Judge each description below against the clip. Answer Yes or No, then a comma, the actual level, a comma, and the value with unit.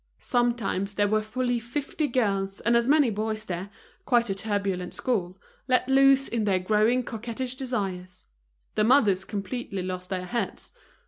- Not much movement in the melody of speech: No, average, 4.1 semitones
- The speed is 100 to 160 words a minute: Yes, average, 150 wpm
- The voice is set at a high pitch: Yes, high, 215 Hz